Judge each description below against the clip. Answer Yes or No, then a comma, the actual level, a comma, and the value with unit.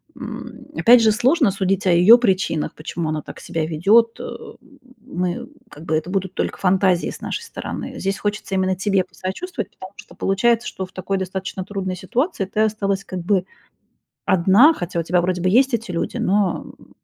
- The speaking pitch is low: No, high, 190 Hz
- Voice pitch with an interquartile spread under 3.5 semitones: Yes, average, 2.9 semitones